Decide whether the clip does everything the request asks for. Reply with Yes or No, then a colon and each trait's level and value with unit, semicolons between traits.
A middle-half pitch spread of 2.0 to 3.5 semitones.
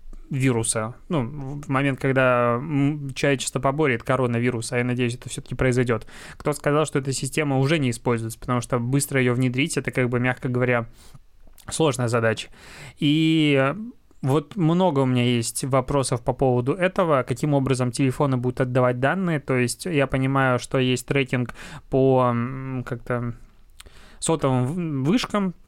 Yes: narrow, 2.5 semitones